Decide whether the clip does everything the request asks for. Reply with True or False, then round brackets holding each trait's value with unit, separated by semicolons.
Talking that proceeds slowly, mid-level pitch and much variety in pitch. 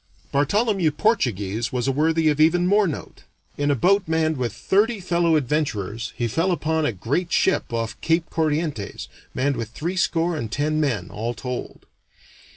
False (160 wpm; 155 Hz; 6.1 semitones)